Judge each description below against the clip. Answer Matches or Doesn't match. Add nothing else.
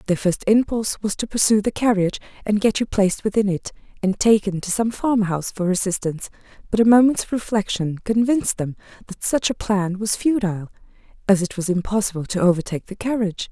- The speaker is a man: Doesn't match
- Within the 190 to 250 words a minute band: Doesn't match